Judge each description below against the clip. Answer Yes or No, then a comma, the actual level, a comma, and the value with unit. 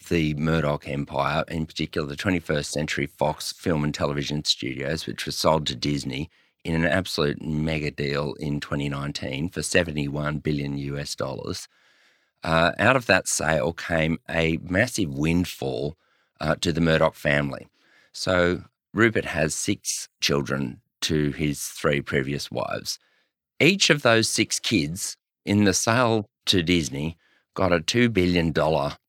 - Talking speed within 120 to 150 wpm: Yes, average, 140 wpm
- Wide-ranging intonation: No, average, 3.4 semitones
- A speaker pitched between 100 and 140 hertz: No, very low, 80 Hz